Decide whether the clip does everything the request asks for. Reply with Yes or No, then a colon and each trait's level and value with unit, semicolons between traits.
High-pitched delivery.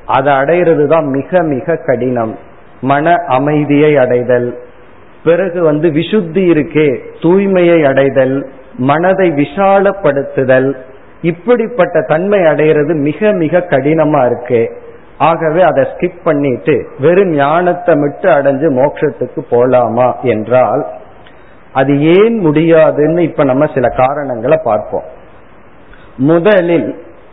No: medium, 155 Hz